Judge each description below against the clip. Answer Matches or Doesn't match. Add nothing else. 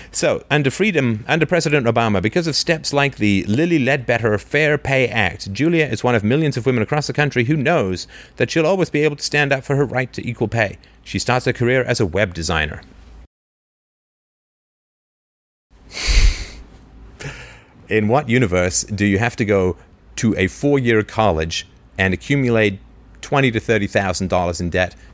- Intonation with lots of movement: Matches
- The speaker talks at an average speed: Matches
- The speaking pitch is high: Doesn't match